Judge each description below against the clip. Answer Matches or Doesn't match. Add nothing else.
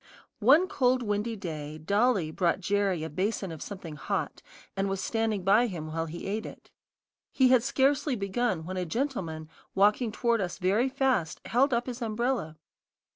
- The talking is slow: Doesn't match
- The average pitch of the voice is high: Matches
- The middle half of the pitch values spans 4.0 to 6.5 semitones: Matches